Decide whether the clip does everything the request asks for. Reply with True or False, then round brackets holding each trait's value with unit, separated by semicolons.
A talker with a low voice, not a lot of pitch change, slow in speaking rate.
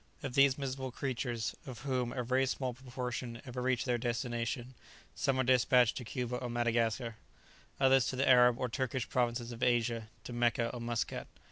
False (125 Hz; 1.6 semitones; 175 wpm)